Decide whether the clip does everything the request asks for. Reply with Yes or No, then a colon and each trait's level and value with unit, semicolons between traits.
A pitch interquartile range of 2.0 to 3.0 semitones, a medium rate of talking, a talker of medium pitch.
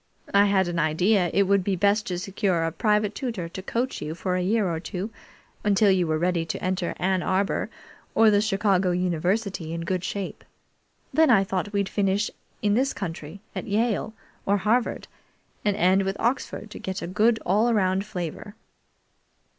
No: narrow, 2.6 semitones; average, 180 wpm; high, 195 Hz